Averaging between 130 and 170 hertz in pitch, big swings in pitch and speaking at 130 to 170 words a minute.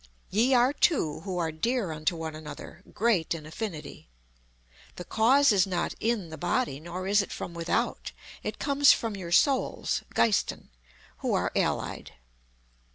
No: high, 190 Hz; wide, 6.3 semitones; average, 155 wpm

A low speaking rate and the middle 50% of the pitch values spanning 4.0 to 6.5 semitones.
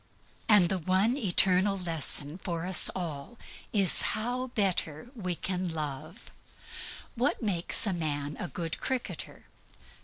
Yes: slow, 125 wpm; average, 4.3 semitones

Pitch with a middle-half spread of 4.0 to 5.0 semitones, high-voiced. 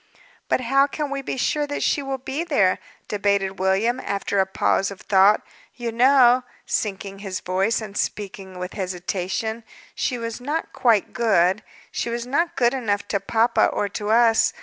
Yes: average, 4.5 semitones; high, 220 Hz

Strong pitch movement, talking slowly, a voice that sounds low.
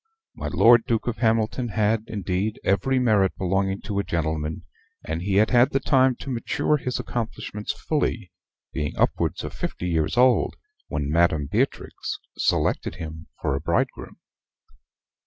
No: wide, 6.0 semitones; average, 150 wpm; low, 100 Hz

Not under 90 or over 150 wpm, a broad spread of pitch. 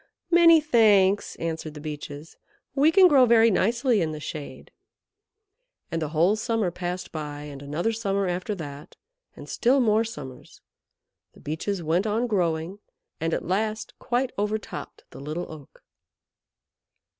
Yes: average, 145 wpm; wide, 6.3 semitones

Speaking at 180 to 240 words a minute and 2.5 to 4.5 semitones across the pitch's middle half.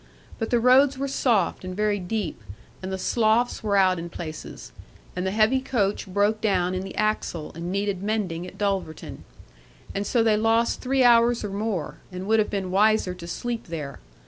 Yes: average, 190 wpm; average, 3.5 semitones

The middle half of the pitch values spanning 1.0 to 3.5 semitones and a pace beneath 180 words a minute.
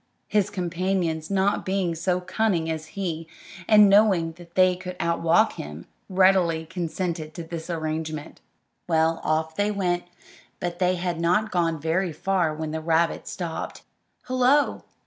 Yes: average, 2.8 semitones; average, 140 wpm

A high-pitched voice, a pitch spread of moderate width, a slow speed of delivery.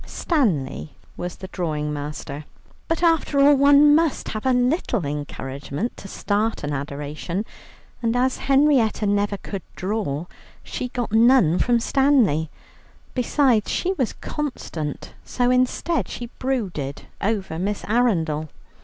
No: high, 215 Hz; wide, 8.7 semitones; slow, 125 wpm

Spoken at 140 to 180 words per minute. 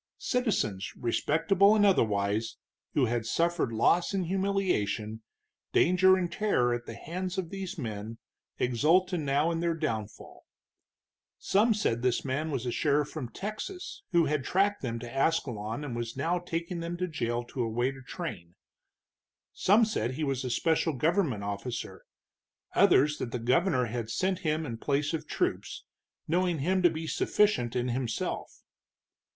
Yes: average, 155 wpm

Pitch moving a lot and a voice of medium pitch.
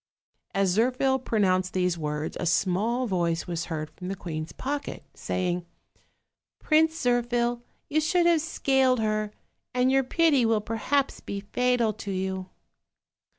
No: wide, 5.9 semitones; high, 220 Hz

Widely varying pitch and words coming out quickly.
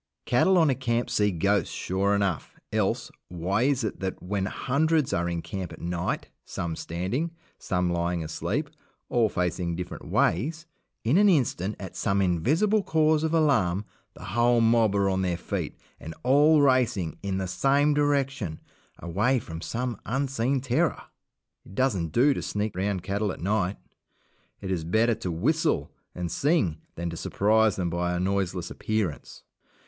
No: wide, 6.7 semitones; average, 165 wpm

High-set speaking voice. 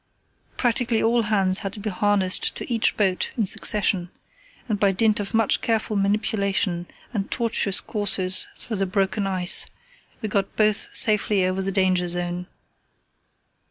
Yes: high, 200 Hz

